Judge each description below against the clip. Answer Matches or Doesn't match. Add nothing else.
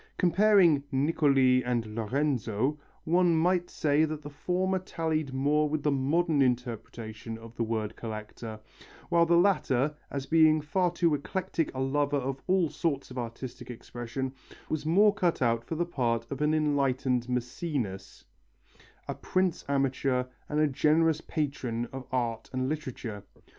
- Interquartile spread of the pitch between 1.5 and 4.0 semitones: Doesn't match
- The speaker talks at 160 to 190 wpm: Doesn't match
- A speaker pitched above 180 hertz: Doesn't match